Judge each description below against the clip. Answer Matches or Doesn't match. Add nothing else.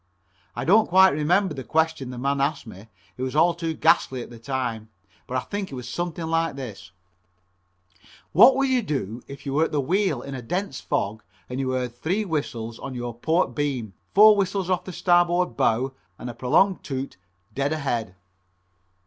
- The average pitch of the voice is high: Doesn't match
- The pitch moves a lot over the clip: Matches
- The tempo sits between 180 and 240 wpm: Matches